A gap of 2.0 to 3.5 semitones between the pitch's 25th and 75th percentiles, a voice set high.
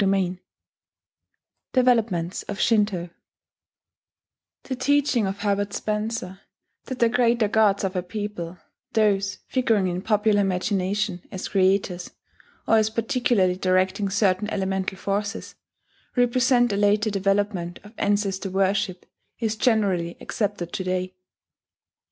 Yes: average, 2.7 semitones; high, 205 Hz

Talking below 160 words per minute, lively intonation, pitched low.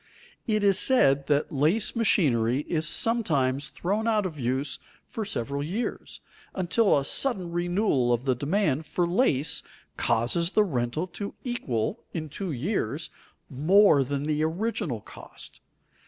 No: average, 140 wpm; wide, 6.7 semitones; medium, 155 Hz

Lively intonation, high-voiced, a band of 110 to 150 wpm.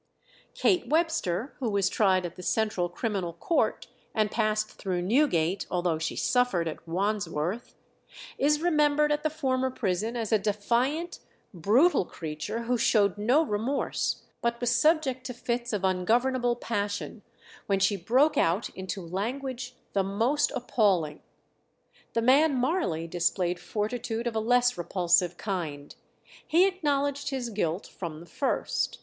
Yes: wide, 6.0 semitones; high, 220 Hz; average, 140 wpm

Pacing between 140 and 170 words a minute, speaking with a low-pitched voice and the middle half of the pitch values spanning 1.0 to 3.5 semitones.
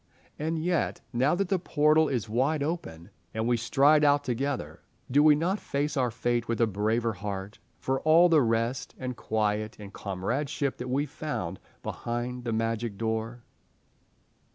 No: average, 160 wpm; low, 125 Hz; average, 4.8 semitones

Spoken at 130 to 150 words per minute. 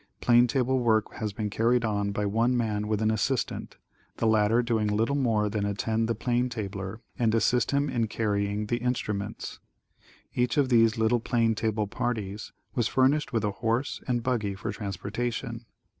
No: average, 175 wpm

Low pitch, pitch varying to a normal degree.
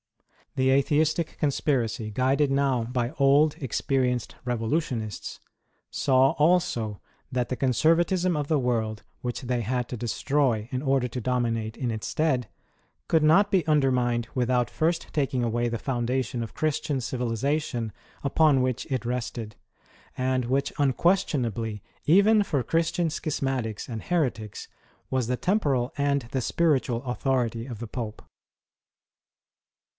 Yes: low, 130 Hz; average, 3.7 semitones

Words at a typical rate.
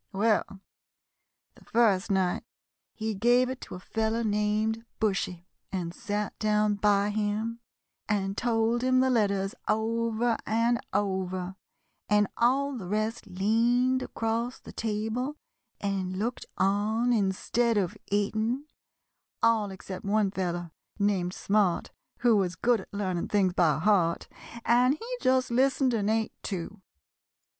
No: slow, 130 wpm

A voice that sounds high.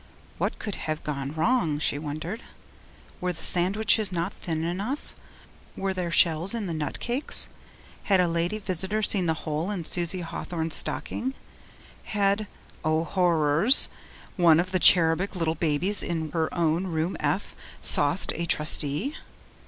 No: medium, 175 Hz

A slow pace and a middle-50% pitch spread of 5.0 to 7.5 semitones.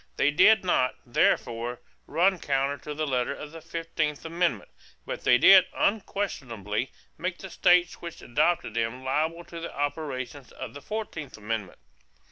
No: average, 150 wpm; average, 5.3 semitones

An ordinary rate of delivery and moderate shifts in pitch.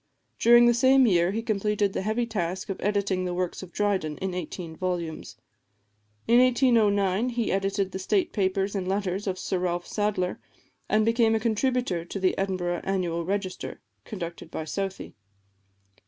Yes: average, 160 wpm; average, 3.1 semitones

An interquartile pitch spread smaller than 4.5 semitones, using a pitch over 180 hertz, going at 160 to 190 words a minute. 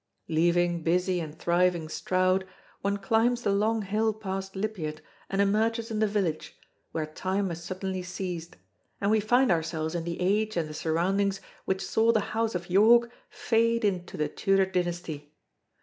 Yes: average, 3.8 semitones; high, 190 Hz; average, 165 wpm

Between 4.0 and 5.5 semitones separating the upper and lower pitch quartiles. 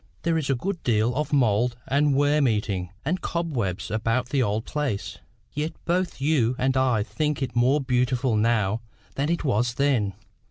Yes: average, 4.5 semitones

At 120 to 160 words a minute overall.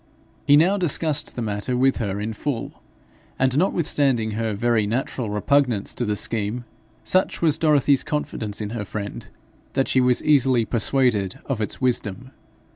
Yes: average, 155 wpm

